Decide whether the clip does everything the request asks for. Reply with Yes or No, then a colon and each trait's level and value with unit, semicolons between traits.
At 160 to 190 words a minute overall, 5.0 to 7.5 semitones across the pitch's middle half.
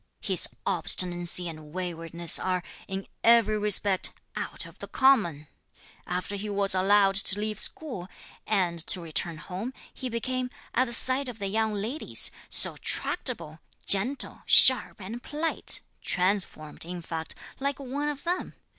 No: average, 145 wpm; wide, 5.6 semitones